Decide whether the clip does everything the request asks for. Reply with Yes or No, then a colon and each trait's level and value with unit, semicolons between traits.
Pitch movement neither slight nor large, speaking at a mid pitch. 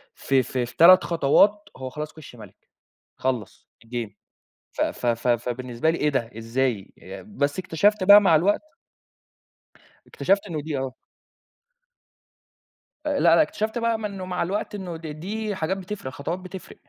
No: wide, 7.1 semitones; medium, 160 Hz